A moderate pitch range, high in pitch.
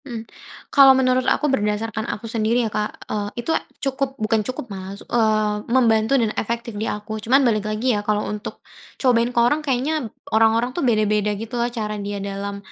Yes: average, 3.1 semitones; high, 225 Hz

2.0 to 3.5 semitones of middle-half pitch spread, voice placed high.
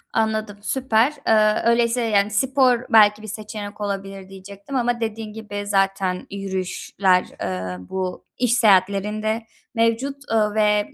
Yes: narrow, 2.4 semitones; high, 210 Hz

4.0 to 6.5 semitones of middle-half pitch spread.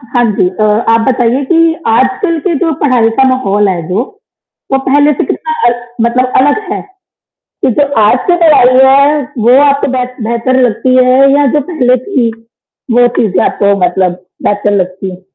Yes: average, 4.5 semitones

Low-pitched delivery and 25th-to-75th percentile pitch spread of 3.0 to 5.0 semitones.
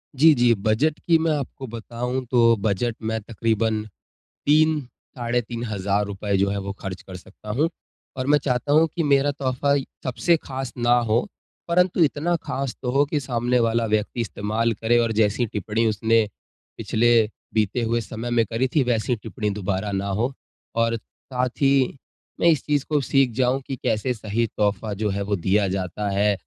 Yes: low, 115 Hz; average, 3.9 semitones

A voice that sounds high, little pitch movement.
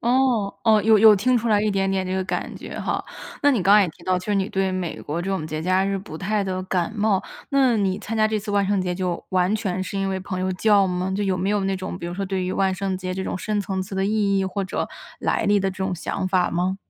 Yes: high, 195 Hz; narrow, 1.9 semitones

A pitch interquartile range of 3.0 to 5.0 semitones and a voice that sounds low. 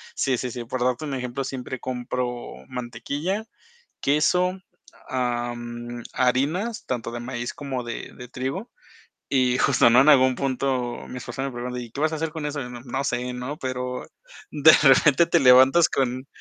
No: narrow, 2.4 semitones; low, 130 Hz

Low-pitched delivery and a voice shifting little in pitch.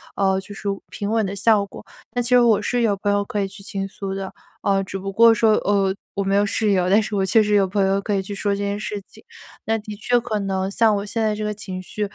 No: high, 205 Hz; narrow, 1.6 semitones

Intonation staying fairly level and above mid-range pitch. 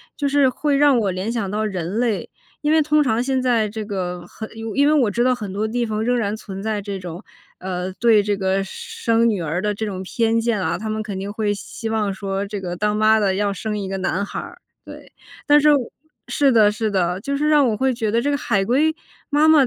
No: average, 4.1 semitones; high, 215 Hz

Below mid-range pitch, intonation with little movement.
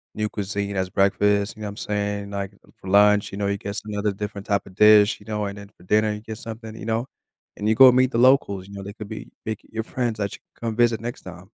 Yes: low, 105 Hz; narrow, 1.7 semitones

